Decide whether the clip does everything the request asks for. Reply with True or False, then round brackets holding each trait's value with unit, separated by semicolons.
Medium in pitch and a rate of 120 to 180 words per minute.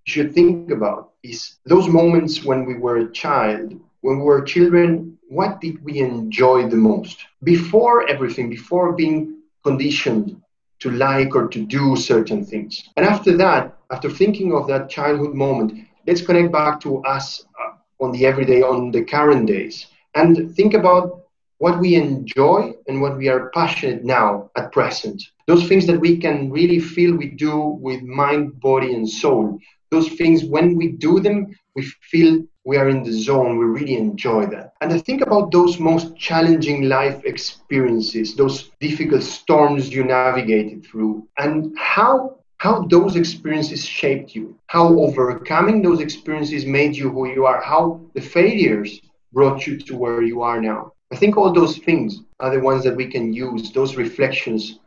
True (150 Hz; 170 wpm)